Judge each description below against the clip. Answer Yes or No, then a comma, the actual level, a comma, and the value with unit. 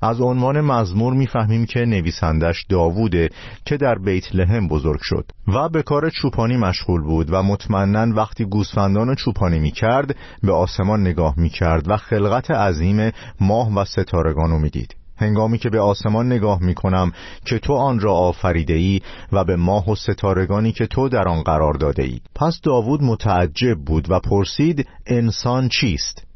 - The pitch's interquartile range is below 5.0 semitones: Yes, average, 4.6 semitones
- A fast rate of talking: Yes, fast, 165 wpm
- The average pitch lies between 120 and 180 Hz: No, low, 100 Hz